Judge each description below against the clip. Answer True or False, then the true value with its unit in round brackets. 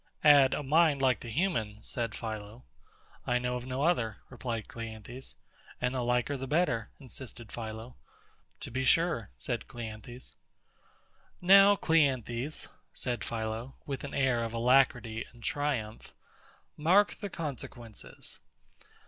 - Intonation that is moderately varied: True (3.8 semitones)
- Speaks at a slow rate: True (130 wpm)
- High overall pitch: False (125 Hz)